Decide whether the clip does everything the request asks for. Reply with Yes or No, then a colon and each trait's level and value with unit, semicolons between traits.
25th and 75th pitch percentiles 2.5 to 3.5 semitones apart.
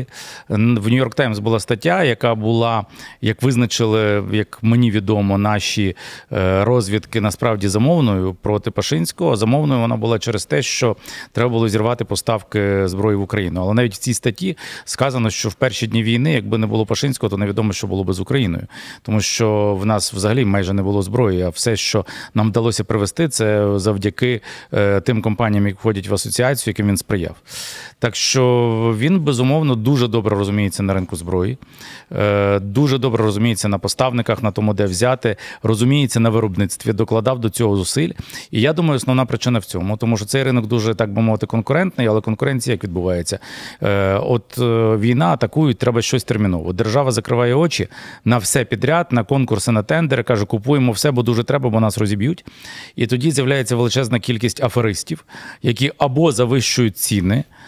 Yes: average, 3.1 semitones